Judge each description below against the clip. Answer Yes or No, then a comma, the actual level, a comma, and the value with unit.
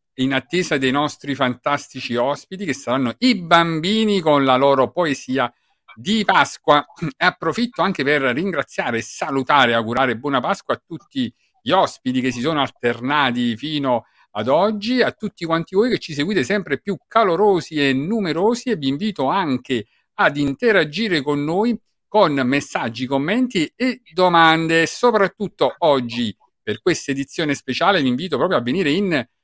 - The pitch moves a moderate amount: No, wide, 7.5 semitones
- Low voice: No, medium, 160 Hz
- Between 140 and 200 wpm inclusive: Yes, average, 150 wpm